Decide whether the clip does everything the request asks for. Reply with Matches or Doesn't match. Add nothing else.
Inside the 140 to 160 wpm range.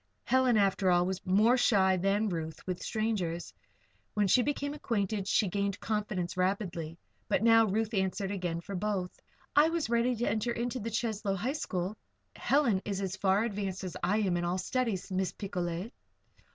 Doesn't match